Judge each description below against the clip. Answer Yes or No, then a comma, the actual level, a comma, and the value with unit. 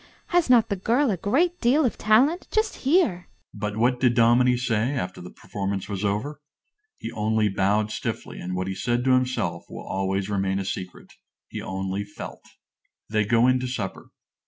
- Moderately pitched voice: No, low, 120 Hz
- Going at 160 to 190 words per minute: Yes, average, 180 wpm